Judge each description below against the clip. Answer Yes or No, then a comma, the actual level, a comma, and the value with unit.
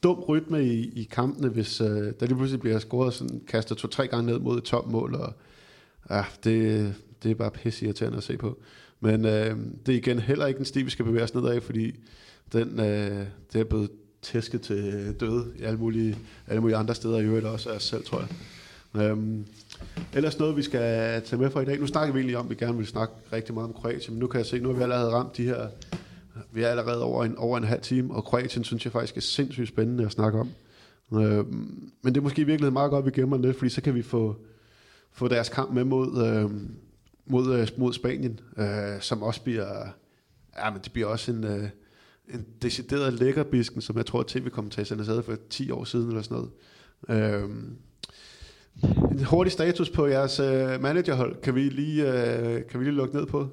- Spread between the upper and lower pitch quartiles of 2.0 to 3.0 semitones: Yes, average, 2.7 semitones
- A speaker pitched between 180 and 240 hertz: No, low, 120 Hz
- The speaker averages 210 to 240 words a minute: Yes, average, 220 wpm